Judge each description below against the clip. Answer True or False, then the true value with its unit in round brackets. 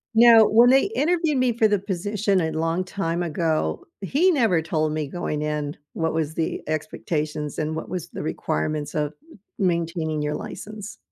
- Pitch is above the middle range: False (165 Hz)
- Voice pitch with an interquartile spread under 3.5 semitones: False (5.3 semitones)